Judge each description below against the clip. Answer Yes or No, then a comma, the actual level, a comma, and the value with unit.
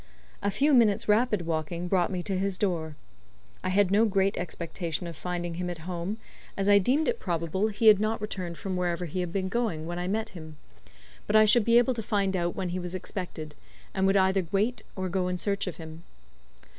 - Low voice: No, medium, 185 Hz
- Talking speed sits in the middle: No, fast, 220 wpm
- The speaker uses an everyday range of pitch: Yes, average, 3.0 semitones